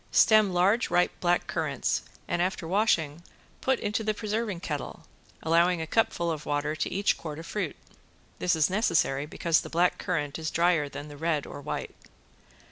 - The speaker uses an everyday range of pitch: Yes, average, 4.2 semitones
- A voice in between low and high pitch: Yes, medium, 170 Hz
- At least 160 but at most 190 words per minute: Yes, average, 175 wpm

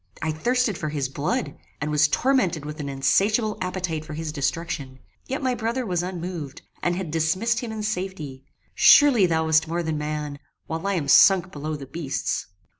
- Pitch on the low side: No, medium, 165 Hz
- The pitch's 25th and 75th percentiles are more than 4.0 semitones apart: Yes, average, 4.4 semitones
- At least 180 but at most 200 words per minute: Yes, average, 185 wpm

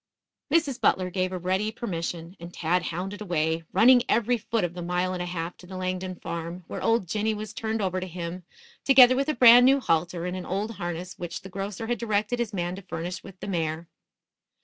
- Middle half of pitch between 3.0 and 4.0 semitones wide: Yes, average, 3.7 semitones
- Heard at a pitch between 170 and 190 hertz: Yes, medium, 185 Hz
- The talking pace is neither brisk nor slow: No, fast, 215 wpm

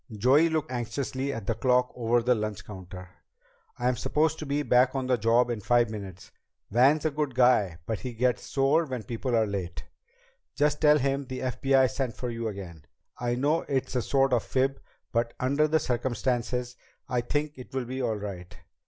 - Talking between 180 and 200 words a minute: Yes, average, 190 wpm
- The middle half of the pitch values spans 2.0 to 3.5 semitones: Yes, average, 2.9 semitones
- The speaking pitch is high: No, low, 125 Hz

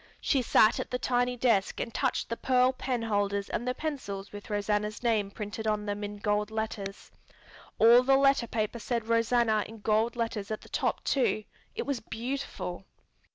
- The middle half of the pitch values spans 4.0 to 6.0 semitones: No, average, 3.0 semitones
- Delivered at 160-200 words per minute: Yes, average, 175 wpm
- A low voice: No, high, 225 Hz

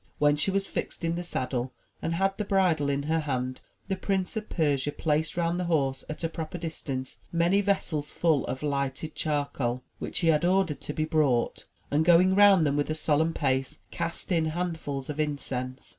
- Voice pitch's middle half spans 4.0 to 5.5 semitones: No, average, 3.6 semitones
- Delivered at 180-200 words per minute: Yes, average, 195 wpm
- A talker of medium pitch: Yes, medium, 155 Hz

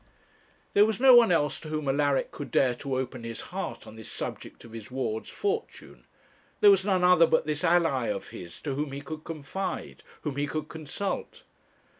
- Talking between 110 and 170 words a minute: No, average, 195 wpm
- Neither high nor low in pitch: Yes, medium, 150 Hz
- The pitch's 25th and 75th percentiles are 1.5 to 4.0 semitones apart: No, average, 5.3 semitones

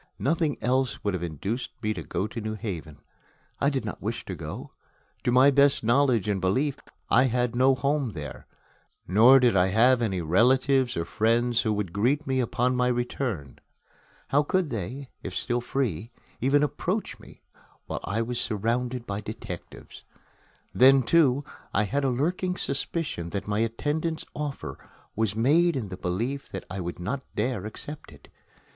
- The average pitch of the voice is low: Yes, low, 120 Hz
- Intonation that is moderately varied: Yes, average, 4.9 semitones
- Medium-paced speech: Yes, average, 170 wpm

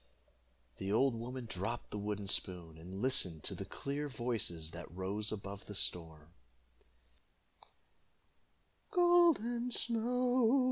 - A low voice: Yes, low, 110 Hz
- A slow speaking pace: Yes, slow, 110 wpm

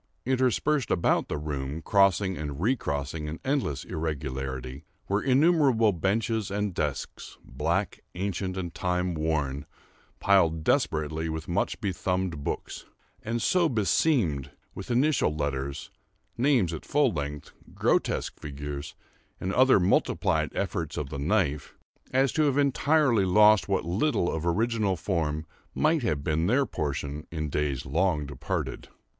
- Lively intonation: Yes, wide, 7.2 semitones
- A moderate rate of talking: No, slow, 130 wpm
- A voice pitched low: Yes, very low, 90 Hz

